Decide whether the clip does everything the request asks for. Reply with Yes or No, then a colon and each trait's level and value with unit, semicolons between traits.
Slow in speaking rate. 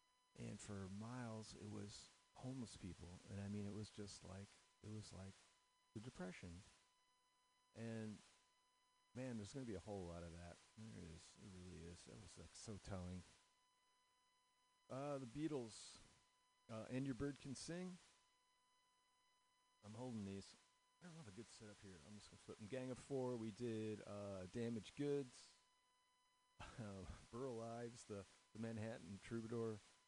No: average, 160 wpm